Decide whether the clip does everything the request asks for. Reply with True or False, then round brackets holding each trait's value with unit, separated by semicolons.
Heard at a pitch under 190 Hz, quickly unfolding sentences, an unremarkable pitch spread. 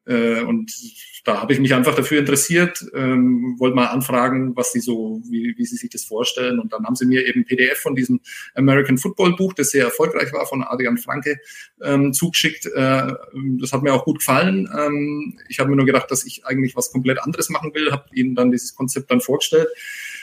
True (135 Hz; 210 wpm; 4.3 semitones)